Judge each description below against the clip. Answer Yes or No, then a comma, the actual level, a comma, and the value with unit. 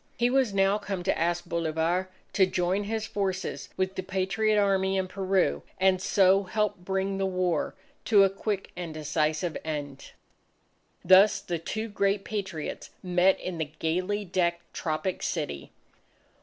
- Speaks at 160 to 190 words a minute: No, average, 145 wpm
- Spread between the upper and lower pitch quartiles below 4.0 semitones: Yes, narrow, 2.4 semitones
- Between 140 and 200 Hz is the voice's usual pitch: Yes, medium, 185 Hz